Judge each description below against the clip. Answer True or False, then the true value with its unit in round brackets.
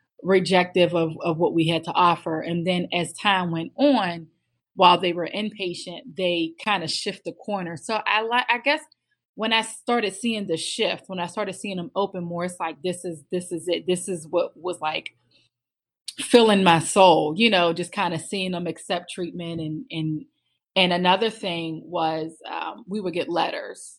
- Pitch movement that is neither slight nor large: True (3.2 semitones)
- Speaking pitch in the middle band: True (180 Hz)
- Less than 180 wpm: False (195 wpm)